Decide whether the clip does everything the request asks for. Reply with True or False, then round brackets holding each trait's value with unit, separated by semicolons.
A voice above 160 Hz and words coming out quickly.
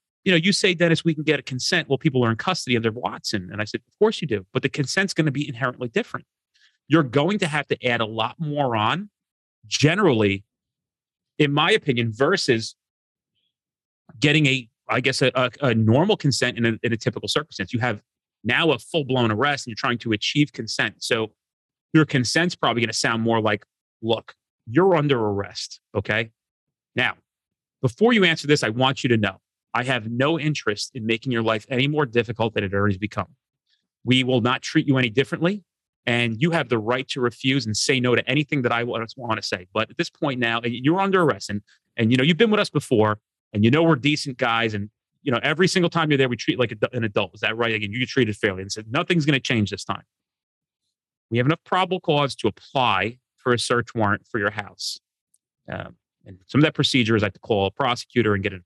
False (125 Hz; 225 wpm)